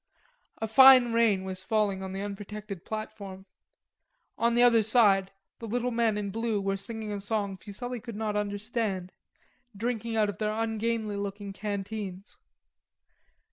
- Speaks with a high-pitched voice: Yes, high, 210 Hz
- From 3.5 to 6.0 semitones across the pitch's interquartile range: No, narrow, 2.4 semitones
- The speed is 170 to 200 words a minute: No, average, 145 wpm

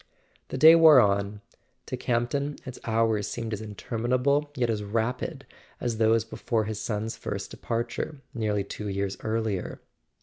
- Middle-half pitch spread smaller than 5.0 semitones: Yes, average, 3.1 semitones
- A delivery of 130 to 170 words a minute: Yes, average, 145 wpm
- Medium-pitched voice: No, low, 115 Hz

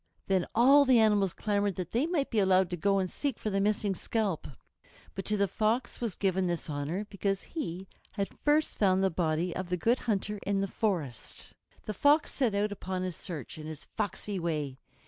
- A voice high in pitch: Yes, high, 195 Hz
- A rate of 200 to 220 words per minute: Yes, fast, 205 wpm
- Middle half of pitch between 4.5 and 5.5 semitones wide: No, average, 3.2 semitones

